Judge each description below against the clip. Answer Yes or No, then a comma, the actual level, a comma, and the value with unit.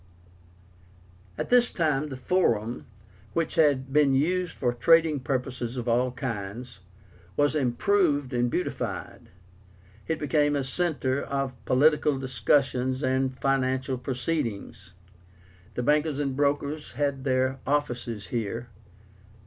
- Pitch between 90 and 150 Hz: Yes, low, 135 Hz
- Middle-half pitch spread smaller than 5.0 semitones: Yes, average, 3.0 semitones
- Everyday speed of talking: No, slow, 115 wpm